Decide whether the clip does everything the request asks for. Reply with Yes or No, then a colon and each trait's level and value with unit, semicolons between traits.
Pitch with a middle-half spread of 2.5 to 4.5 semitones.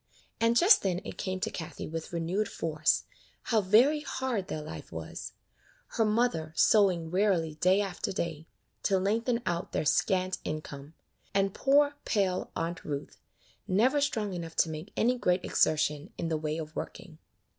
No: average, 5.2 semitones